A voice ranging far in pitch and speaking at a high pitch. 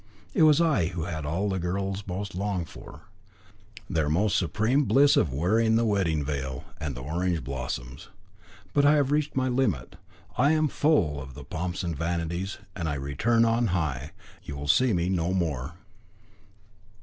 No: wide, 6.9 semitones; very low, 90 Hz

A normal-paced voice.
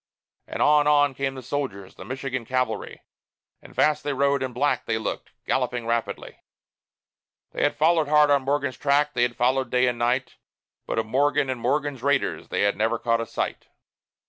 Yes: average, 185 wpm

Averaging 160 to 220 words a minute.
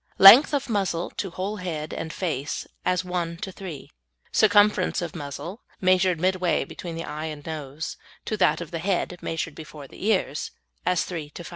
Yes: average, 180 wpm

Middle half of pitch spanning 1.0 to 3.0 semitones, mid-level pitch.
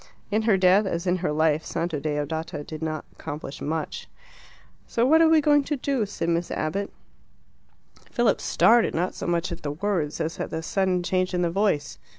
No: average, 4.5 semitones; medium, 175 Hz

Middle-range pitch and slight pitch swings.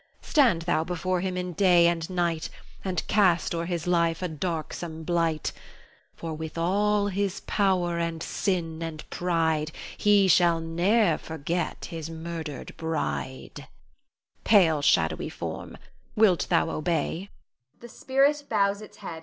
Yes: medium, 170 Hz; narrow, 2.2 semitones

